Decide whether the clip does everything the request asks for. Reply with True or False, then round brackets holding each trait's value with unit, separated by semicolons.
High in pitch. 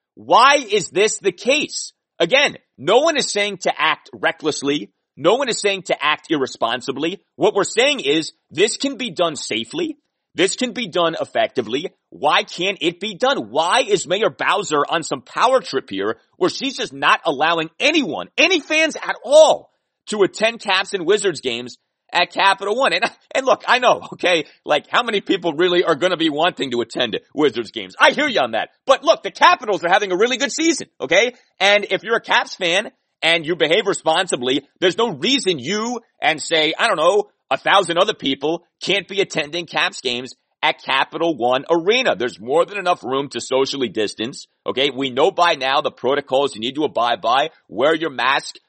True (195 Hz)